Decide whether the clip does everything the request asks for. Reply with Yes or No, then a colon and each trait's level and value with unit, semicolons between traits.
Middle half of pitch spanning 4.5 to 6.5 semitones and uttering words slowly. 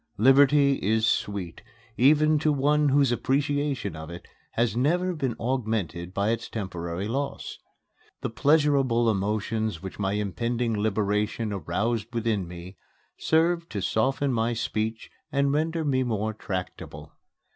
Yes: average, 5.3 semitones; slow, 130 wpm